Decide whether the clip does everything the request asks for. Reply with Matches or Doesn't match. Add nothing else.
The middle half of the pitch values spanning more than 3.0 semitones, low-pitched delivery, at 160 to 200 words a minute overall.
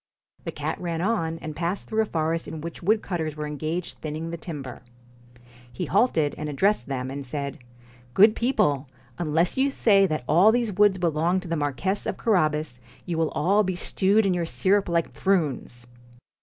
Doesn't match